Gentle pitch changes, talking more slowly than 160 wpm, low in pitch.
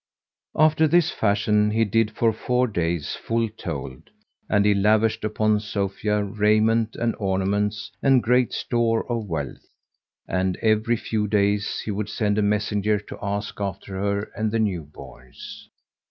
Yes: narrow, 1.9 semitones; average, 150 wpm; low, 105 Hz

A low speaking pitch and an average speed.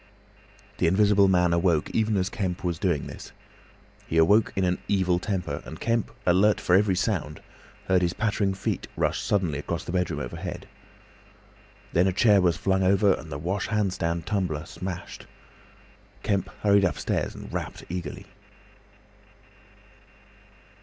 Yes: very low, 95 Hz; average, 145 wpm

